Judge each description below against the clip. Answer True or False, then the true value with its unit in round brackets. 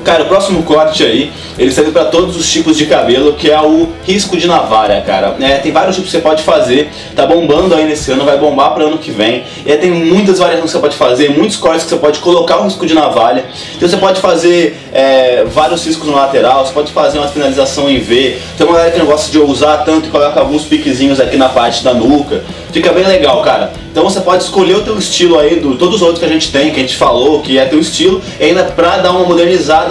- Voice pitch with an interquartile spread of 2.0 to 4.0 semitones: True (3.3 semitones)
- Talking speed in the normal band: False (255 wpm)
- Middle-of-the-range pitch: True (160 Hz)